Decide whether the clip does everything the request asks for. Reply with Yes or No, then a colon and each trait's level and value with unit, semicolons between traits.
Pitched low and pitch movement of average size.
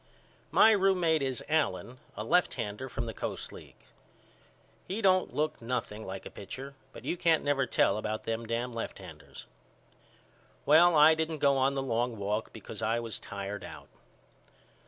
No: low, 130 Hz; wide, 5.9 semitones